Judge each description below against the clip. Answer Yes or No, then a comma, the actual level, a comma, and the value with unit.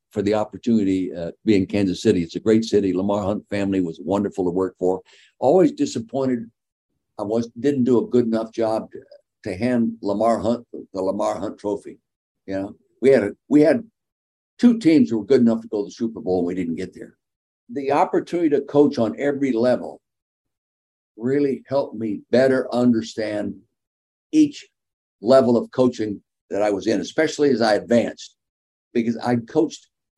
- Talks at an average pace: Yes, average, 185 wpm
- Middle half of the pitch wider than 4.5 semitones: Yes, average, 5.0 semitones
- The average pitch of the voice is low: Yes, low, 115 Hz